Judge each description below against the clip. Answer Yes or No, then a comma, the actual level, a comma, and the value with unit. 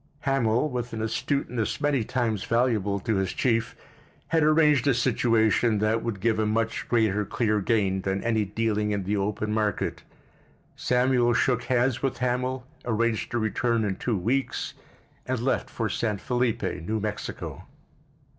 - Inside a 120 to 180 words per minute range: Yes, average, 155 wpm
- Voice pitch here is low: Yes, low, 115 Hz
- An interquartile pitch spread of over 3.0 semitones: No, average, 2.7 semitones